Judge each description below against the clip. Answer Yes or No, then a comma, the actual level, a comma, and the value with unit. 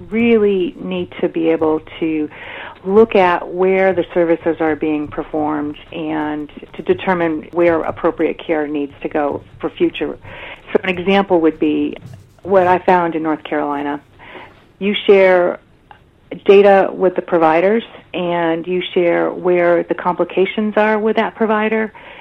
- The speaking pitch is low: No, medium, 175 Hz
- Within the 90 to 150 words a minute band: Yes, average, 140 wpm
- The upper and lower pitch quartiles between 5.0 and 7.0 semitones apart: No, average, 3.4 semitones